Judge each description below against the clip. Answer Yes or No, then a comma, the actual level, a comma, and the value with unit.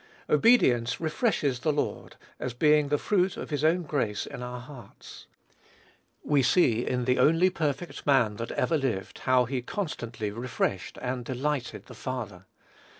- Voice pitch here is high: No, low, 130 Hz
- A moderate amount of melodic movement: Yes, average, 3.8 semitones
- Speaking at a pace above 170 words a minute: No, average, 150 wpm